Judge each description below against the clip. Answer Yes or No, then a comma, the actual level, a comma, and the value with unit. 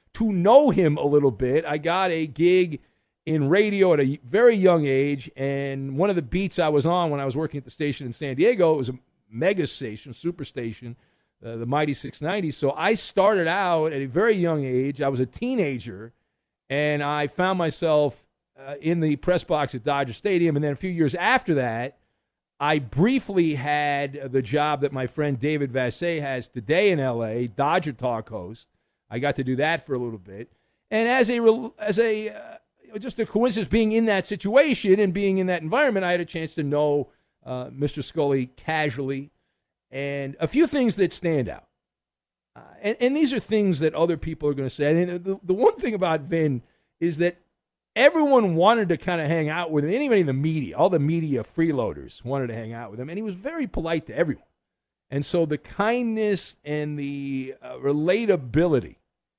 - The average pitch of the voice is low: No, medium, 155 Hz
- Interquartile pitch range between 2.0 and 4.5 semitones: No, average, 5.3 semitones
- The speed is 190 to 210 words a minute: Yes, average, 200 wpm